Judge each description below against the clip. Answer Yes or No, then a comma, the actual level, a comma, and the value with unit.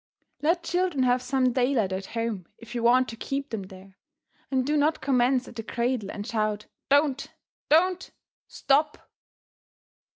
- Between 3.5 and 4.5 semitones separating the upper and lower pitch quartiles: Yes, average, 4.0 semitones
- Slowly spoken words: No, average, 155 wpm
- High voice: Yes, very high, 255 Hz